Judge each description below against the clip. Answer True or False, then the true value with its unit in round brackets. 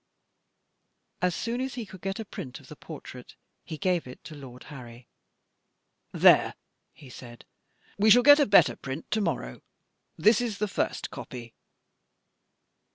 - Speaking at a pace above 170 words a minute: False (155 wpm)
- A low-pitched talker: False (175 Hz)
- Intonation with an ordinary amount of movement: False (9.0 semitones)